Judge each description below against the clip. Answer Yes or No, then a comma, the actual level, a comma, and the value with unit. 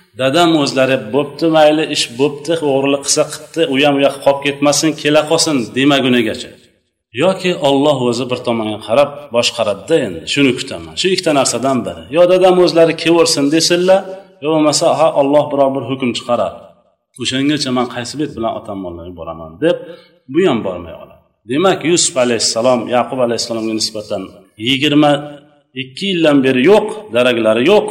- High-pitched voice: No, medium, 140 Hz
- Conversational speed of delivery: Yes, average, 150 wpm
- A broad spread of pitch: No, average, 4.5 semitones